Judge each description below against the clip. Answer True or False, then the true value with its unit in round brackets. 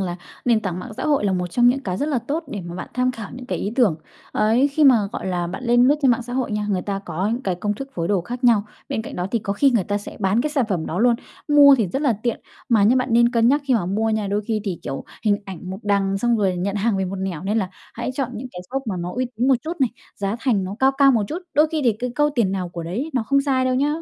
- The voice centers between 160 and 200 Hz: False (225 Hz)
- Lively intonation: False (4.8 semitones)